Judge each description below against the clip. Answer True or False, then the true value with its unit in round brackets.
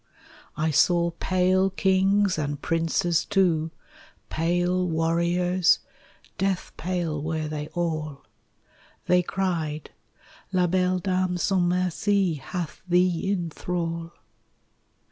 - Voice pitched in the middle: True (175 Hz)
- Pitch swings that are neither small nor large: False (2.2 semitones)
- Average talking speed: False (100 wpm)